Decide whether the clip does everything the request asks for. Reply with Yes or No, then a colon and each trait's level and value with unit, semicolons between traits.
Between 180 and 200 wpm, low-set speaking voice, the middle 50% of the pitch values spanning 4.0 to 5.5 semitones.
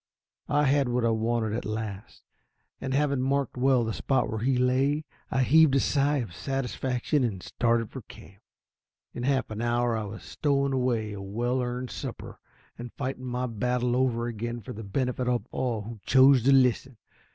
No: average, 185 wpm; low, 125 Hz; narrow, 2.6 semitones